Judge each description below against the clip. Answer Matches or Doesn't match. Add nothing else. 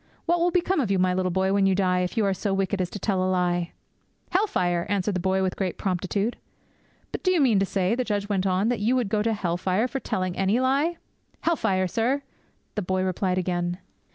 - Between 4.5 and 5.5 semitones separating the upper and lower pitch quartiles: Doesn't match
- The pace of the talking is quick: Matches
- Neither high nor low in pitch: Doesn't match